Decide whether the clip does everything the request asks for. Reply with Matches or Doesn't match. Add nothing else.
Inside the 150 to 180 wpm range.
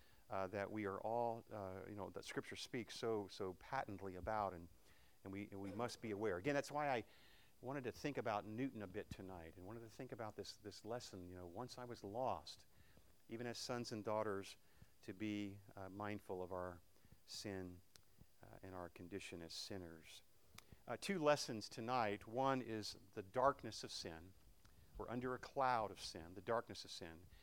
Doesn't match